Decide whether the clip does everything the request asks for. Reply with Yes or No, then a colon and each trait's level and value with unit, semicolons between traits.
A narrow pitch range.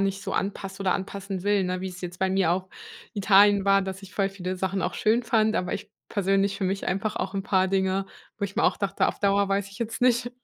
Yes: narrow, 1.1 semitones